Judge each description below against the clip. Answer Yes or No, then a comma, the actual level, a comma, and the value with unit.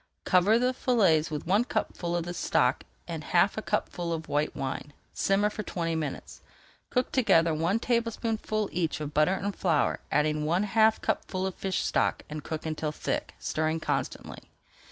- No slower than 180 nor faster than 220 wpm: No, average, 170 wpm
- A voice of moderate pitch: Yes, medium, 175 Hz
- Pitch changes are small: No, average, 5.0 semitones